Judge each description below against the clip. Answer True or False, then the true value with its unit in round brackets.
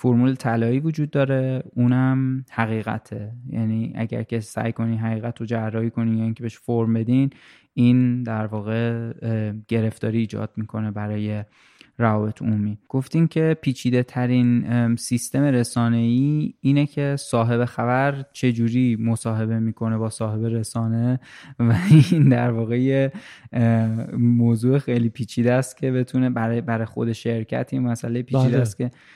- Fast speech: False (135 wpm)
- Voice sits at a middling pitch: False (120 Hz)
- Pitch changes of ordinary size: False (2.2 semitones)